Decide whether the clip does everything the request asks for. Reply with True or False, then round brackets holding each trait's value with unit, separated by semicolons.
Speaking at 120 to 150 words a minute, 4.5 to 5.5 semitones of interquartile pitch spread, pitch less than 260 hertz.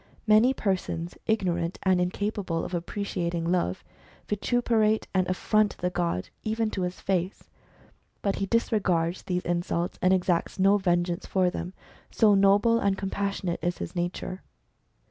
False (145 wpm; 2.8 semitones; 185 Hz)